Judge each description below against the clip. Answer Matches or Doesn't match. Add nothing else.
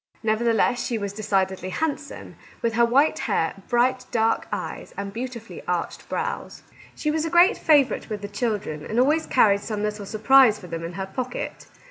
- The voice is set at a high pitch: Matches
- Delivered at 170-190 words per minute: Matches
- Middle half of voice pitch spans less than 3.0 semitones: Doesn't match